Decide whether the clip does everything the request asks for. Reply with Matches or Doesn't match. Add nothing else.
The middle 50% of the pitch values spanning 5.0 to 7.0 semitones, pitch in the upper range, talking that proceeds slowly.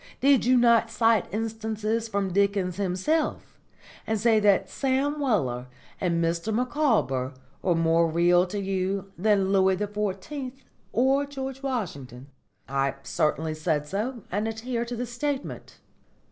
Matches